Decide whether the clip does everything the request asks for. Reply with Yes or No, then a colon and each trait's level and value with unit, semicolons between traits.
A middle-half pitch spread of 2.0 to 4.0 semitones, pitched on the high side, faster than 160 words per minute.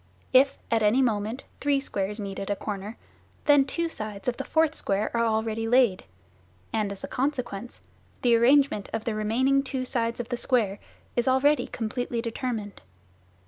Yes: average, 3.6 semitones; high, 235 Hz; average, 170 wpm